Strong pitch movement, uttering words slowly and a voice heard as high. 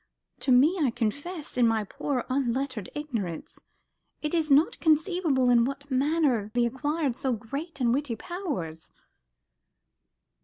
No: average, 4.3 semitones; slow, 130 wpm; very high, 270 Hz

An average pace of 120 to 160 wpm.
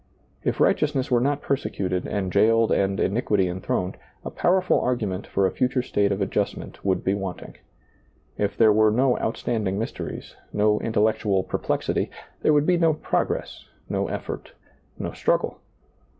Yes: average, 150 wpm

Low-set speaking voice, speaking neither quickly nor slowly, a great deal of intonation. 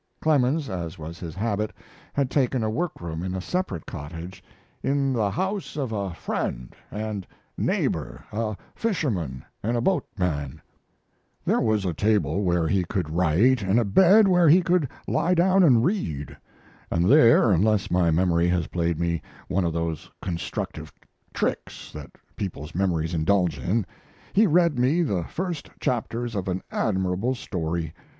Yes: low, 100 Hz; average, 155 wpm; wide, 7.5 semitones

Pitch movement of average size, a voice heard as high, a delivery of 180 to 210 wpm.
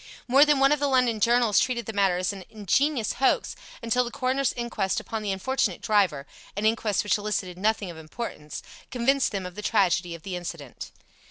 Yes: average, 4.8 semitones; high, 215 Hz; average, 195 wpm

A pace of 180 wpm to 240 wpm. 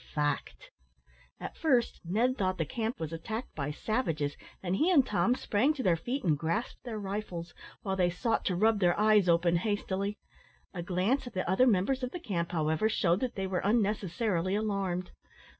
Yes: average, 185 wpm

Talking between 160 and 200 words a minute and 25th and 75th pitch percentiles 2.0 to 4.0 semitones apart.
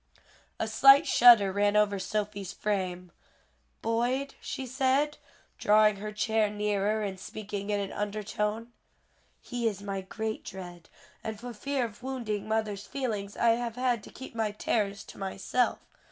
No: average, 150 wpm; average, 2.8 semitones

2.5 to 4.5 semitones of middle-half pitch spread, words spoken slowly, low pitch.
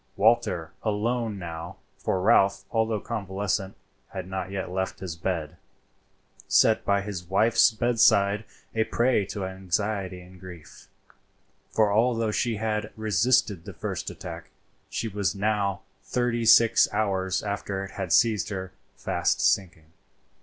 Yes: average, 2.8 semitones; slow, 125 wpm; low, 100 Hz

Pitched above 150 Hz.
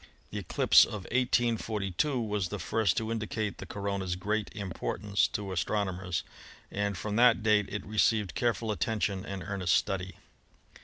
No: low, 105 Hz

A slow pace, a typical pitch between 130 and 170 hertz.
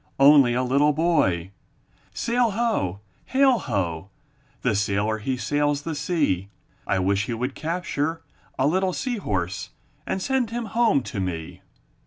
No: average, 145 wpm; medium, 140 Hz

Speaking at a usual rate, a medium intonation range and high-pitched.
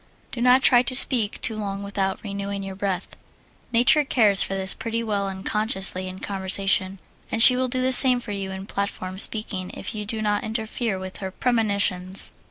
Yes: average, 185 wpm; average, 3.1 semitones; high, 200 Hz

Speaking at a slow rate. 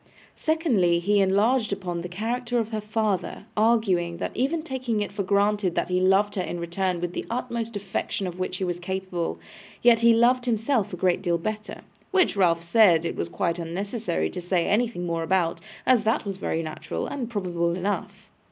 No: average, 190 wpm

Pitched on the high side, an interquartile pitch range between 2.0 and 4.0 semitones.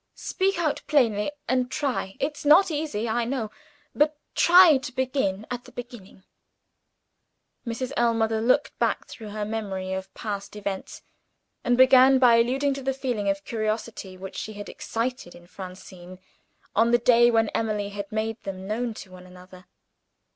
No: high, 225 Hz; average, 4.4 semitones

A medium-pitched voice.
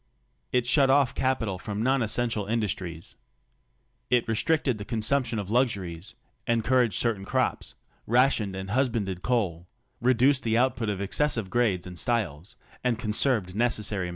No: low, 115 Hz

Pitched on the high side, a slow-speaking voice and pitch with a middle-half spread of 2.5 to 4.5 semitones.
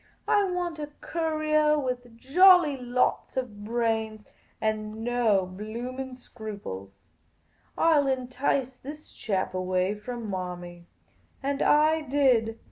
No: high, 245 Hz; slow, 115 wpm; average, 5.3 semitones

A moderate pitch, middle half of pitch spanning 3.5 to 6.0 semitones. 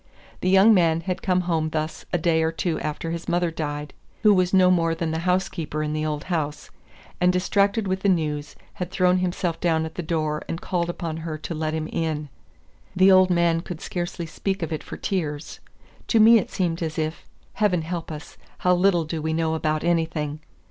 No: medium, 165 Hz; narrow, 2.5 semitones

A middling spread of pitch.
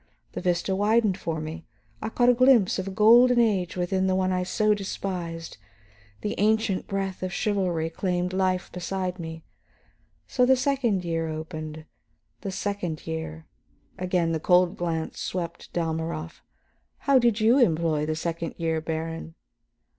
Yes: average, 3.8 semitones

